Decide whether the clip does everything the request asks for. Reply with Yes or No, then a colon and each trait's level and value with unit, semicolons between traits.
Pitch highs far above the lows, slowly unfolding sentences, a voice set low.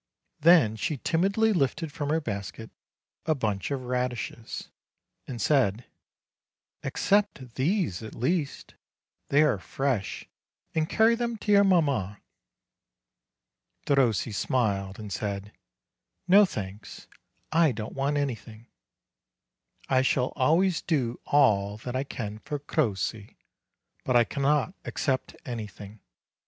Yes: wide, 6.2 semitones; slow, 115 wpm; low, 130 Hz